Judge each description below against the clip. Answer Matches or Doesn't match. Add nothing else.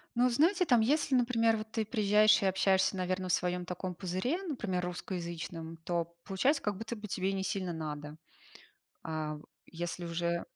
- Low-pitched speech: Doesn't match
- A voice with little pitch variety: Doesn't match